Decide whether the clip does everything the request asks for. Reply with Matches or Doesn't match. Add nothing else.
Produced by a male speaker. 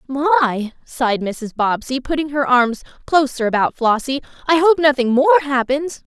Doesn't match